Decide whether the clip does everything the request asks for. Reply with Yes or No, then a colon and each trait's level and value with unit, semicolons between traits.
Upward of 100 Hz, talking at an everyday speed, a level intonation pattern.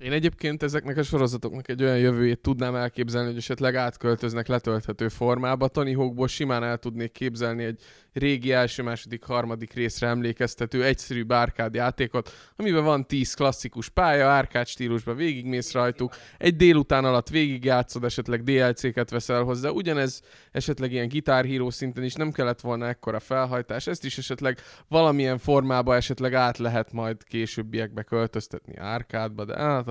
Yes: low, 125 Hz; average, 145 wpm; narrow, 2.1 semitones